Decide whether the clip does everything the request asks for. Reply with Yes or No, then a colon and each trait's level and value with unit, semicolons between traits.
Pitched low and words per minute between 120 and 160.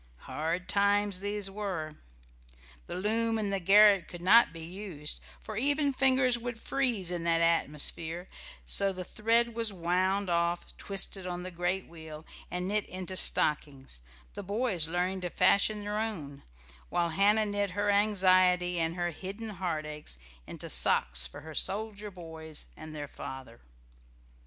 No: medium, 185 Hz; average, 150 wpm